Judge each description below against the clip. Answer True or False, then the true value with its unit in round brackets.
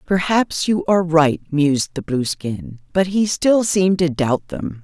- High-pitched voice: False (165 Hz)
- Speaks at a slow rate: False (175 wpm)